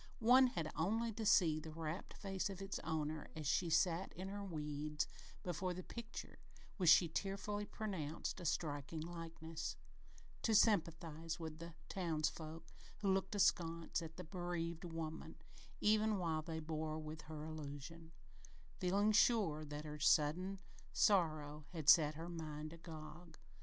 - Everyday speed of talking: Yes, average, 145 wpm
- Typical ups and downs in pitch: Yes, average, 3.3 semitones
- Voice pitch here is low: No, medium, 165 Hz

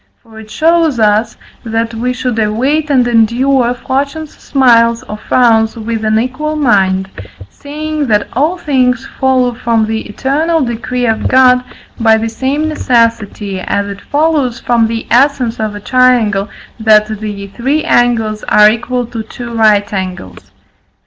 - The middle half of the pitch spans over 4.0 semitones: No, average, 3.2 semitones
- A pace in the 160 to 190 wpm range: No, average, 150 wpm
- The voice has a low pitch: No, high, 235 Hz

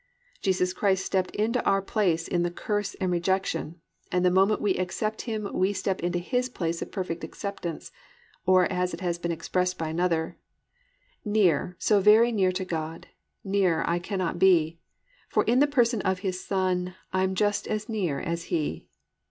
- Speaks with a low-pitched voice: No, medium, 185 Hz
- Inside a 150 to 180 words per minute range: Yes, average, 175 wpm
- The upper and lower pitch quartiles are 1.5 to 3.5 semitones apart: Yes, average, 2.9 semitones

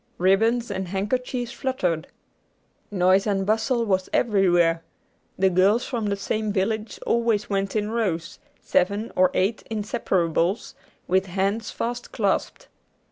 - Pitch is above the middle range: Yes, high, 200 Hz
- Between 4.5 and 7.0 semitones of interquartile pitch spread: No, average, 3.1 semitones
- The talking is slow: Yes, slow, 125 wpm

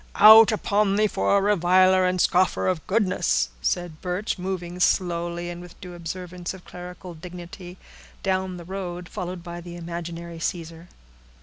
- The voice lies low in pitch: No, medium, 180 Hz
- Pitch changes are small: Yes, narrow, 1.4 semitones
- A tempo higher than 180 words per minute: No, average, 160 wpm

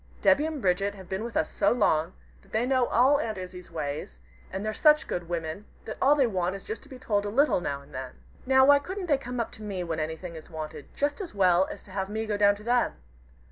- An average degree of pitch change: No, wide, 6.7 semitones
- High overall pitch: Yes, high, 205 Hz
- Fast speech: Yes, fast, 260 wpm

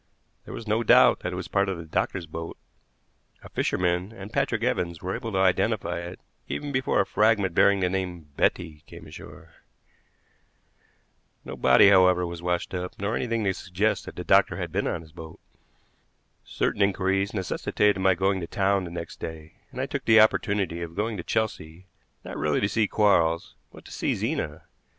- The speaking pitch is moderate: No, very low, 95 Hz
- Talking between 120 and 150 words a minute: No, average, 185 wpm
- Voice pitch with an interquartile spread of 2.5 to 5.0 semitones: Yes, average, 3.1 semitones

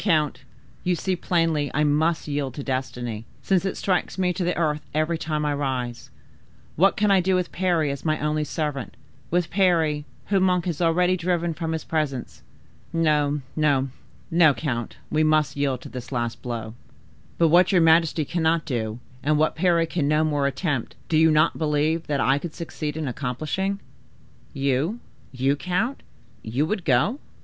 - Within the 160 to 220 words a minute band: Yes, average, 170 wpm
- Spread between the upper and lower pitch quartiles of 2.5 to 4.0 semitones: Yes, average, 3.3 semitones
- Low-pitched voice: No, medium, 155 Hz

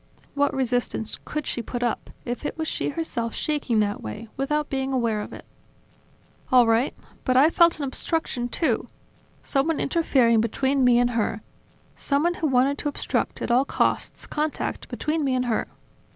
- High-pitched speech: Yes, very high, 265 Hz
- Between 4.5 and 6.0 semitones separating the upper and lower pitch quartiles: No, average, 3.8 semitones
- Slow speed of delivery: No, average, 170 wpm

